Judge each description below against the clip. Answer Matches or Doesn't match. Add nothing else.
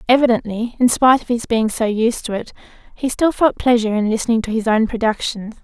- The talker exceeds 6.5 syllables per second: Doesn't match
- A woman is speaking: Matches